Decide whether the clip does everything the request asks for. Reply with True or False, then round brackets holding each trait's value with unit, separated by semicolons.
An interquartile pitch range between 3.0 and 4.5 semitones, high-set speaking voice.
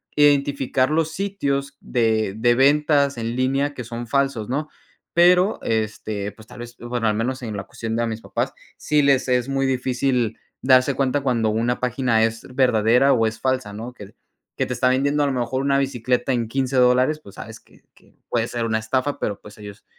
False (3.3 semitones; 125 Hz)